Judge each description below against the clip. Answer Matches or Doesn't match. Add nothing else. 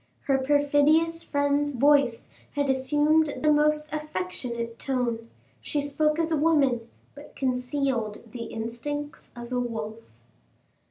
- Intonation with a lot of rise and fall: Doesn't match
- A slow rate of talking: Matches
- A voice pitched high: Matches